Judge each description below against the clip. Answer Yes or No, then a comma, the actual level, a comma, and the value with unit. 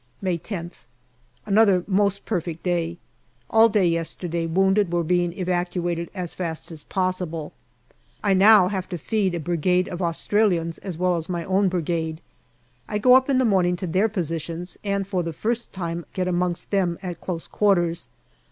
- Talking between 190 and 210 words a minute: No, average, 170 wpm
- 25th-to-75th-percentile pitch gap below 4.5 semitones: Yes, narrow, 2.5 semitones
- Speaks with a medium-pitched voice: Yes, medium, 180 Hz